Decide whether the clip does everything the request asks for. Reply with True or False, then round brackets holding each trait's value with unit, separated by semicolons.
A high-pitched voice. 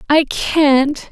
True (290 Hz)